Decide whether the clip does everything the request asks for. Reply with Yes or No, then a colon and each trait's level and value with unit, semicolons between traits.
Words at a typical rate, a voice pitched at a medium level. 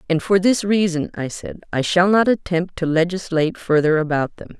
Yes: average, 195 wpm; medium, 175 Hz